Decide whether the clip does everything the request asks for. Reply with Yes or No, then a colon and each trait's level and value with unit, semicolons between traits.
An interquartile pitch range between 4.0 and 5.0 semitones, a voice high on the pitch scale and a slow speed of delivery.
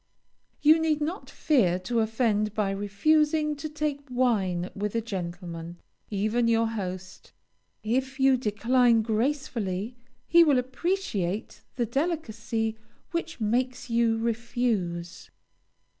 Yes: average, 4.6 semitones; high, 230 Hz; slow, 115 wpm